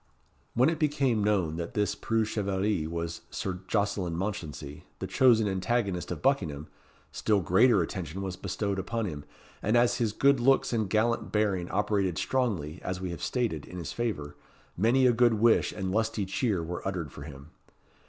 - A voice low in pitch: Yes, low, 100 Hz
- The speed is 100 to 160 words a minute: No, average, 175 wpm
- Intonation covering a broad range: No, average, 4.8 semitones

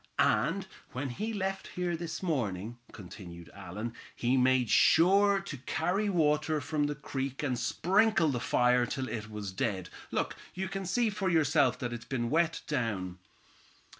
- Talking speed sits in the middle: Yes, average, 160 wpm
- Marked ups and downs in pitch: Yes, wide, 6.8 semitones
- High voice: No, medium, 145 Hz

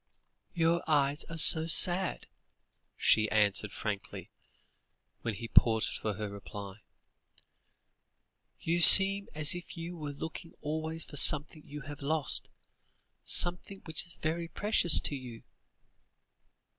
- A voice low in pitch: No, medium, 155 Hz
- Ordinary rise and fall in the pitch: No, wide, 6.4 semitones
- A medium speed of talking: No, slow, 120 wpm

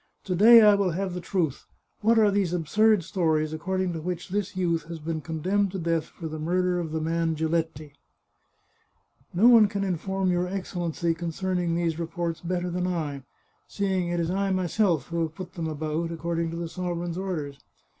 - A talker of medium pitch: Yes, medium, 175 Hz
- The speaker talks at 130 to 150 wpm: No, average, 195 wpm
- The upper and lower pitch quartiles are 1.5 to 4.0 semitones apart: Yes, narrow, 2.5 semitones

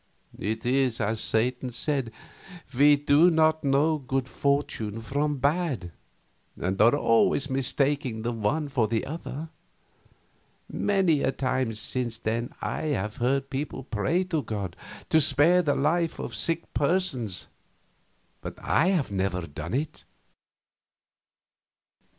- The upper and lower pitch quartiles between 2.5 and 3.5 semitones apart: No, average, 4.8 semitones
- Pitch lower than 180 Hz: Yes, low, 135 Hz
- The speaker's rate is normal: No, slow, 125 wpm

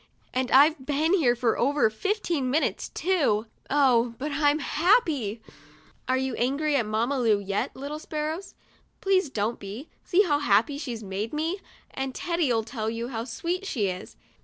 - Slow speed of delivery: No, average, 160 wpm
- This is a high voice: Yes, very high, 270 Hz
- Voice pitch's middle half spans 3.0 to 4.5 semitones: No, average, 5.2 semitones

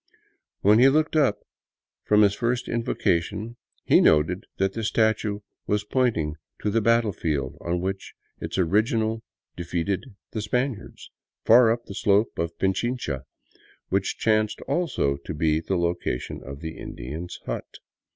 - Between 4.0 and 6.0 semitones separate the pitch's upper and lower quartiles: Yes, average, 5.1 semitones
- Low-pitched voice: Yes, low, 100 Hz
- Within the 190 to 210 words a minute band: No, average, 140 wpm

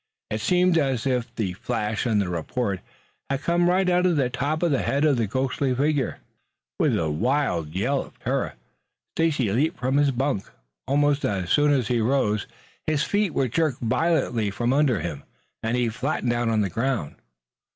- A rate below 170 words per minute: No, average, 190 wpm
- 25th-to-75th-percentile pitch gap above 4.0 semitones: Yes, average, 4.8 semitones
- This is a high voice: No, low, 130 Hz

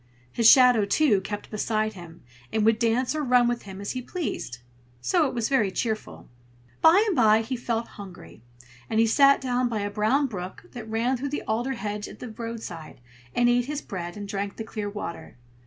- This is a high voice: Yes, high, 225 Hz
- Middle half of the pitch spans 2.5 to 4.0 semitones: Yes, average, 3.4 semitones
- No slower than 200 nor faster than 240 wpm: Yes, fast, 205 wpm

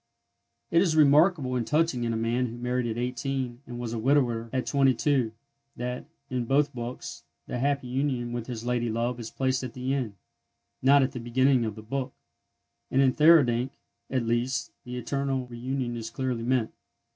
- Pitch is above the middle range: No, low, 125 Hz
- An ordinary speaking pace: Yes, average, 180 wpm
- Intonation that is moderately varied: No, narrow, 2.3 semitones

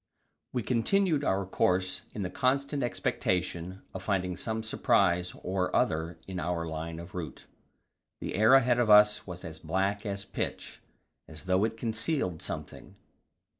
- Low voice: Yes, very low, 95 Hz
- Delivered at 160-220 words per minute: No, average, 150 wpm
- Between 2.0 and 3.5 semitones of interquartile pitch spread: No, average, 4.1 semitones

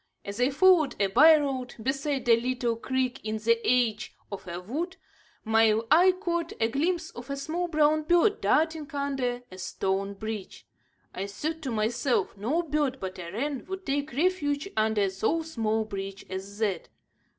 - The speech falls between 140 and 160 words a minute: No, average, 170 wpm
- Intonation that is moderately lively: No, wide, 6.2 semitones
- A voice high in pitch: Yes, very high, 255 Hz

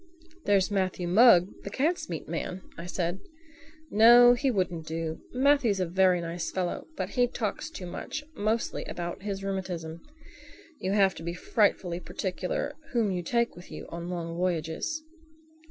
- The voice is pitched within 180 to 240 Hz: Yes, medium, 185 Hz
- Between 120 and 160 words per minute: Yes, average, 155 wpm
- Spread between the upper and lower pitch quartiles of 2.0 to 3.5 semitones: No, average, 4.4 semitones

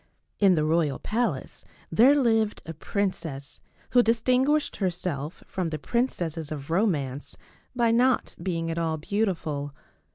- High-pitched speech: No, medium, 175 Hz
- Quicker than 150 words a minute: No, slow, 135 wpm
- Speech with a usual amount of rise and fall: No, wide, 6.6 semitones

